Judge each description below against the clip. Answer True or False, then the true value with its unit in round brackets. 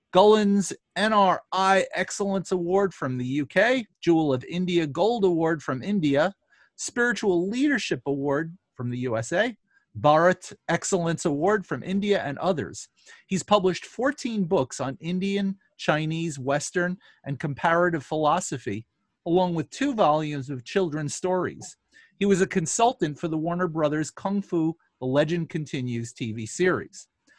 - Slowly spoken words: True (130 wpm)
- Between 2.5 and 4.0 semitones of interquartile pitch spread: False (4.8 semitones)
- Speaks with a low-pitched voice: False (175 Hz)